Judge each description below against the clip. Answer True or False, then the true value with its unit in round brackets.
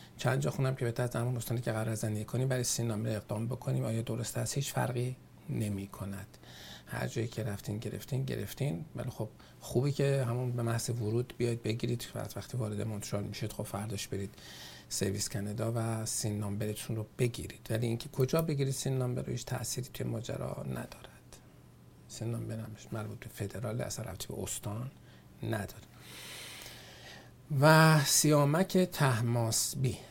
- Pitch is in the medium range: False (115 Hz)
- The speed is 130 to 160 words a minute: True (150 wpm)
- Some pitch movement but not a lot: True (3.0 semitones)